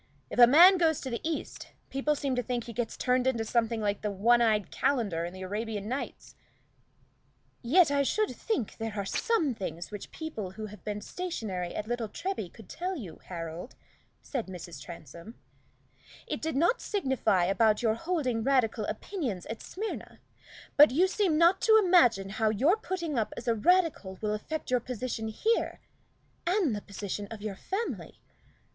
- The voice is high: Yes, high, 235 Hz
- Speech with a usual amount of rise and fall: No, wide, 7.2 semitones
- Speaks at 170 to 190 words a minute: Yes, average, 175 wpm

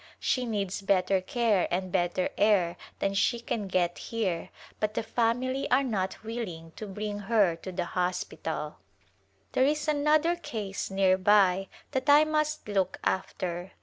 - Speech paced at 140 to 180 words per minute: Yes, average, 150 wpm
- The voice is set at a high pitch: Yes, high, 200 Hz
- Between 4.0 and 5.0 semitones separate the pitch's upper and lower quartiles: Yes, average, 4.4 semitones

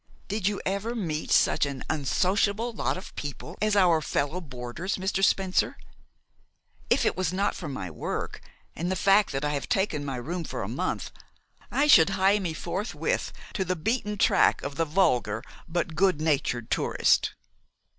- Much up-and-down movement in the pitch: No, average, 5.0 semitones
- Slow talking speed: No, average, 170 wpm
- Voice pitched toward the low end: No, medium, 180 Hz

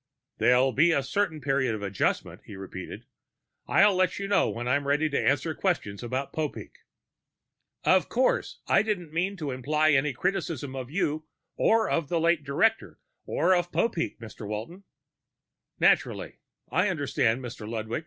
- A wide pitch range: Yes, wide, 5.9 semitones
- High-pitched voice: No, medium, 150 Hz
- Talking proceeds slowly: No, average, 155 wpm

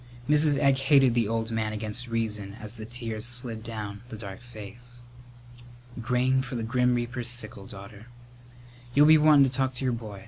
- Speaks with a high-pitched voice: No, low, 120 Hz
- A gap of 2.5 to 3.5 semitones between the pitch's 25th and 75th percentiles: Yes, average, 2.8 semitones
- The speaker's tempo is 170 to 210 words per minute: Yes, average, 180 wpm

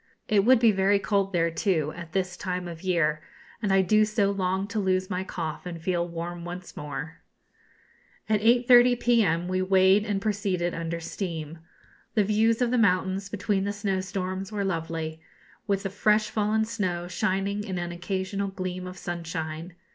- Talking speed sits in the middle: Yes, average, 170 wpm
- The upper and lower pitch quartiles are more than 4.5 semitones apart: No, average, 2.8 semitones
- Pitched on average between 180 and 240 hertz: Yes, high, 190 Hz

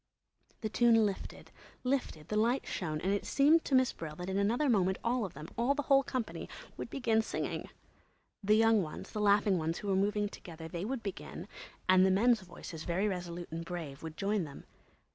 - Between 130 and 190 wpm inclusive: No, average, 200 wpm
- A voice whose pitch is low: No, high, 200 Hz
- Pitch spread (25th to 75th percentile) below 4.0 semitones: No, average, 4.8 semitones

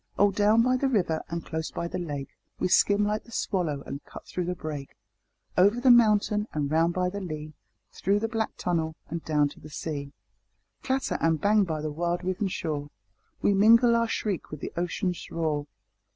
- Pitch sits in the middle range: Yes, medium, 180 Hz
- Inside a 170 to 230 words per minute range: Yes, average, 195 wpm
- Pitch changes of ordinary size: Yes, average, 4.9 semitones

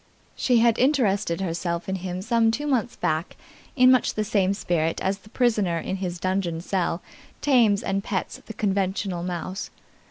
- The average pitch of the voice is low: No, high, 195 Hz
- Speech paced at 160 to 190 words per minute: Yes, average, 165 wpm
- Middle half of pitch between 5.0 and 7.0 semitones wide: No, average, 4.0 semitones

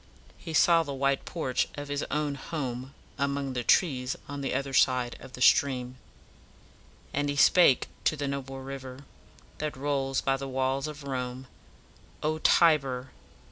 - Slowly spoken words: No, average, 155 wpm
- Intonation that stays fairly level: Yes, narrow, 1.7 semitones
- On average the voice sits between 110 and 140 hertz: Yes, low, 135 Hz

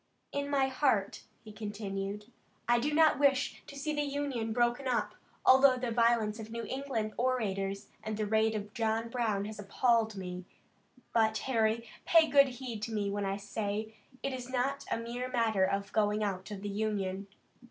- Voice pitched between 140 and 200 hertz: No, high, 225 Hz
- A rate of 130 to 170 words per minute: No, average, 180 wpm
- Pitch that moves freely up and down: No, average, 3.7 semitones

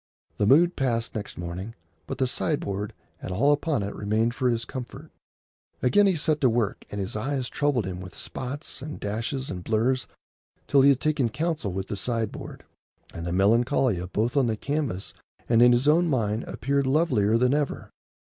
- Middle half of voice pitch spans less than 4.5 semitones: No, average, 5.2 semitones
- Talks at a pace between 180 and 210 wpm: Yes, average, 185 wpm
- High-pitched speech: No, low, 120 Hz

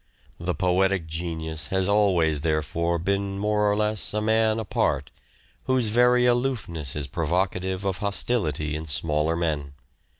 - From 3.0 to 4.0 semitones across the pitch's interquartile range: No, average, 4.7 semitones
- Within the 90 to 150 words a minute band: Yes, average, 140 wpm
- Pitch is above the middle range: No, very low, 90 Hz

